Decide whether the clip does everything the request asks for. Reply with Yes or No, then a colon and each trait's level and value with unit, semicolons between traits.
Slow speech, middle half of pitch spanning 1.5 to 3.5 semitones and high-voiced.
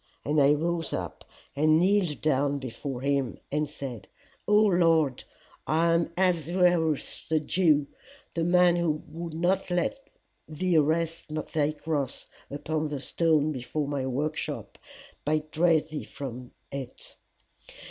No: slow, 130 wpm; average, 2.8 semitones; medium, 155 Hz